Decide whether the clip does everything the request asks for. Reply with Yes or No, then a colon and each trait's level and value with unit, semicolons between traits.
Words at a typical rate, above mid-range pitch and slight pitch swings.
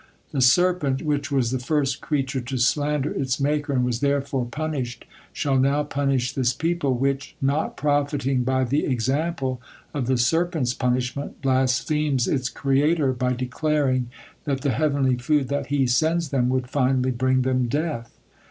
No: average, 155 wpm; low, 135 Hz; narrow, 2.3 semitones